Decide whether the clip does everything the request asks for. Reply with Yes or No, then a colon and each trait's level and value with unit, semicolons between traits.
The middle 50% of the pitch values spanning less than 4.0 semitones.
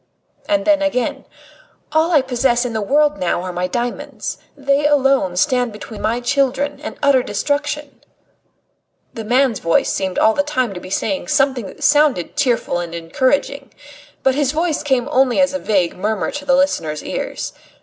No: average, 4.9 semitones